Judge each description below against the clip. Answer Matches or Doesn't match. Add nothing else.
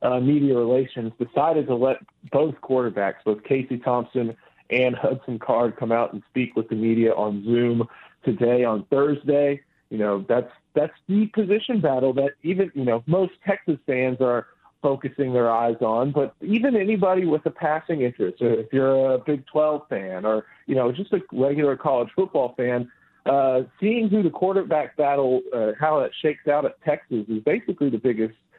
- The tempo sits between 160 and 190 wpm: Matches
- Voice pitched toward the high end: Doesn't match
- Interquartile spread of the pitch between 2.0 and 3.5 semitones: Doesn't match